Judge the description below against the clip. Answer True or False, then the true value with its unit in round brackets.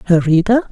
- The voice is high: True (200 Hz)